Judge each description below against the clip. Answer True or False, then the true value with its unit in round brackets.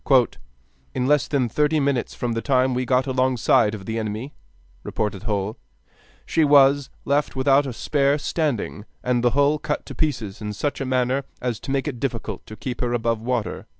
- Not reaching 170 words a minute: False (185 wpm)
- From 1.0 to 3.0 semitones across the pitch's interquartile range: False (3.5 semitones)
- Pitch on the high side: False (130 Hz)